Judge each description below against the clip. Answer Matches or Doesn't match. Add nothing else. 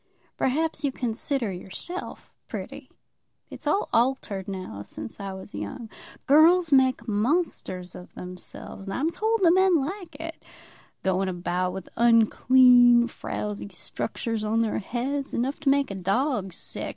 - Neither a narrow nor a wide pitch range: Doesn't match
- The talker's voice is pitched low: Doesn't match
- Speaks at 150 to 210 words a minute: Doesn't match